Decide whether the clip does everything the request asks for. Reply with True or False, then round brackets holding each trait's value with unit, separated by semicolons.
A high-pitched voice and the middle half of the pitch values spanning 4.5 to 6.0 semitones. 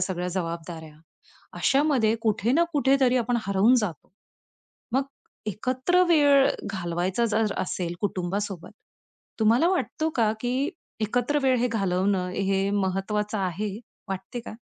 True (215 Hz; 5.2 semitones)